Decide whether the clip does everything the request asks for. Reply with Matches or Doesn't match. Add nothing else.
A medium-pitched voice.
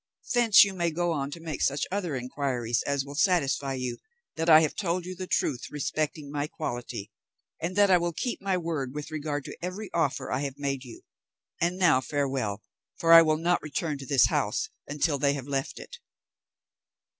Matches